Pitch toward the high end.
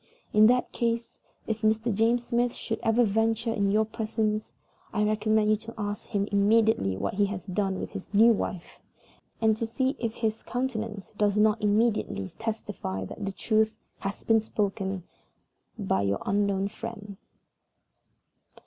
Yes: high, 215 Hz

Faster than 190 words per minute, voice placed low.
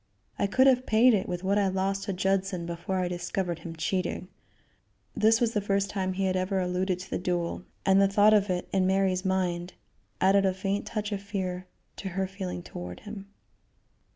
No: average, 200 wpm; high, 190 Hz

